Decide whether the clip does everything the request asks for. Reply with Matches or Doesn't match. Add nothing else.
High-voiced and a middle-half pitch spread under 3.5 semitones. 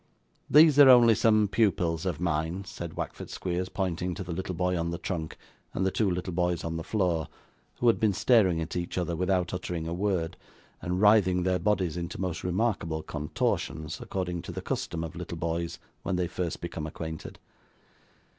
Doesn't match